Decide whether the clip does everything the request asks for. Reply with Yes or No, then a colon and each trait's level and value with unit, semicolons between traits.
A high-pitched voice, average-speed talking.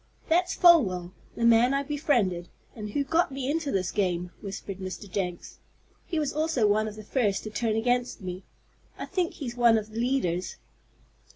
Yes: high, 225 Hz; average, 180 wpm